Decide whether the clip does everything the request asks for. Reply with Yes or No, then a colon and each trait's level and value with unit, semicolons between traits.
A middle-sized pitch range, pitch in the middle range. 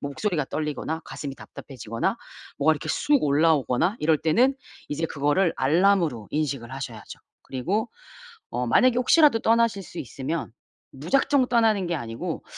No: wide, 7.4 semitones; medium, 160 Hz